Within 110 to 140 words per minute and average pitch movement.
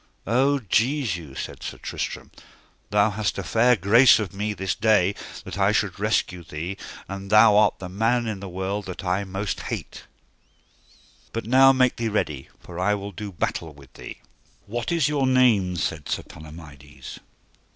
No: average, 170 wpm; average, 4.2 semitones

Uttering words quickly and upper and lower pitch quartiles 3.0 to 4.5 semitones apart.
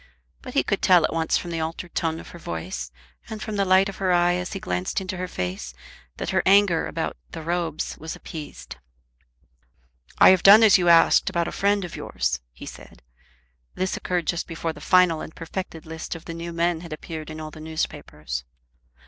No: fast, 210 wpm; narrow, 2.5 semitones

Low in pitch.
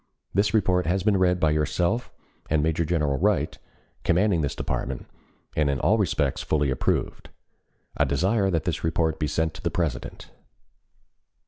Yes: very low, 80 Hz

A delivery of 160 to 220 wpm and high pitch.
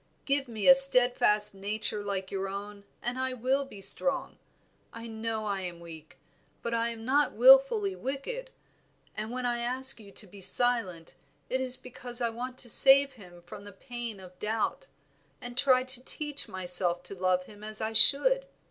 Yes: average, 185 wpm; high, 235 Hz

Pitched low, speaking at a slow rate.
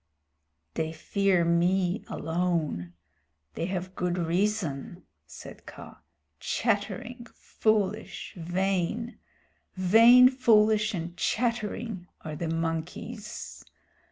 No: medium, 185 Hz; slow, 85 wpm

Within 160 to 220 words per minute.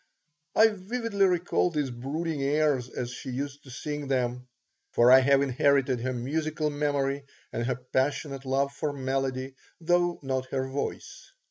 No: average, 150 wpm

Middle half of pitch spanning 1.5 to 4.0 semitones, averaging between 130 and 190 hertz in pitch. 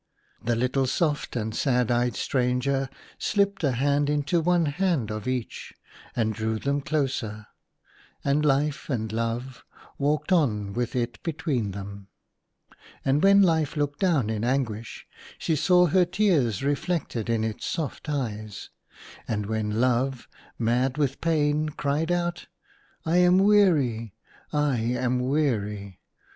No: average, 5.0 semitones; low, 135 Hz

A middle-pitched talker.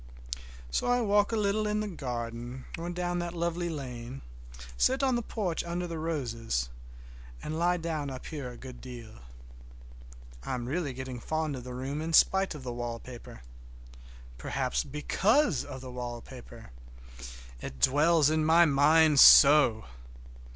Yes: medium, 150 Hz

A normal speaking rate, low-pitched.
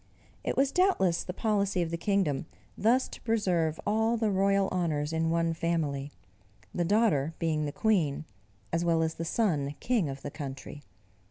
No: average, 170 wpm; medium, 170 Hz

